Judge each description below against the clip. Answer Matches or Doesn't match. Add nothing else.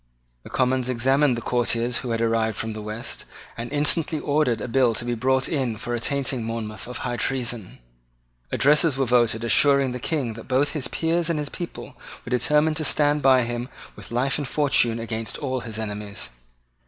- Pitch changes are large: Doesn't match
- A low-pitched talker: Matches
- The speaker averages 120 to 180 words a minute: Doesn't match